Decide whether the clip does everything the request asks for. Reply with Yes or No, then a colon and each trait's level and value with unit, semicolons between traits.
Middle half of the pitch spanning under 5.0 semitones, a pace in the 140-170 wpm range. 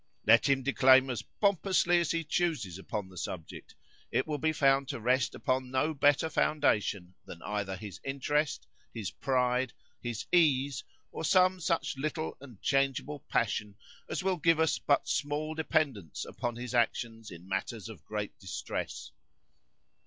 No: wide, 5.6 semitones; average, 155 wpm